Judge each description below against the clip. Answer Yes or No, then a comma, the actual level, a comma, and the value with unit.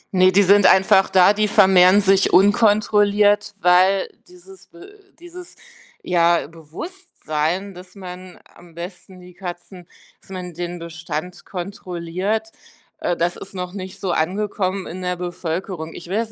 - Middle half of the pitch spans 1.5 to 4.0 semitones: Yes, narrow, 2.5 semitones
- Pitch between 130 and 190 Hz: Yes, medium, 185 Hz